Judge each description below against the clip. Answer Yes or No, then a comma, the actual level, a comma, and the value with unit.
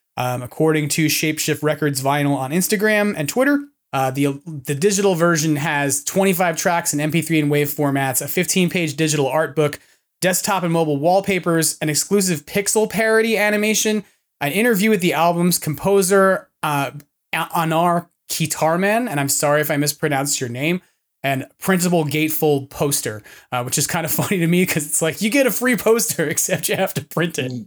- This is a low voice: No, medium, 160 Hz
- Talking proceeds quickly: No, average, 175 wpm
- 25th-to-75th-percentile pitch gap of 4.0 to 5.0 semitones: Yes, average, 4.5 semitones